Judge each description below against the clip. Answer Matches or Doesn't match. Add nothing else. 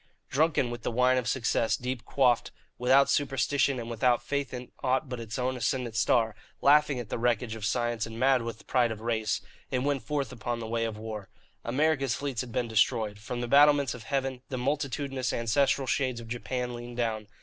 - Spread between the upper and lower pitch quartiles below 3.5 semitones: Matches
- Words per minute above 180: Matches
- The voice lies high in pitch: Doesn't match